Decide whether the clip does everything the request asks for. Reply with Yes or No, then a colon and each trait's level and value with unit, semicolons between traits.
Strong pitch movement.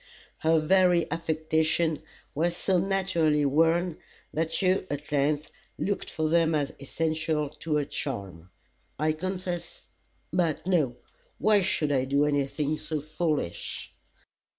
No: average, 2.7 semitones